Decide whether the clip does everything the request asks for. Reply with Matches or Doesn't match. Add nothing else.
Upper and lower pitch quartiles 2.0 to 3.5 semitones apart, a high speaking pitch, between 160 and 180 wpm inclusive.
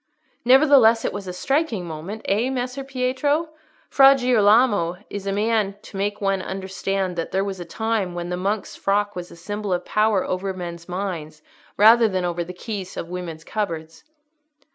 Doesn't match